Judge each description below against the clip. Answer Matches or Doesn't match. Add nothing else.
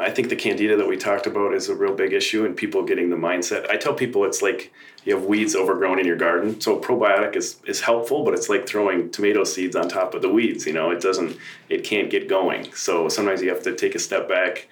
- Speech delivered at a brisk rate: Matches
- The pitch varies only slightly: Matches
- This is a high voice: Matches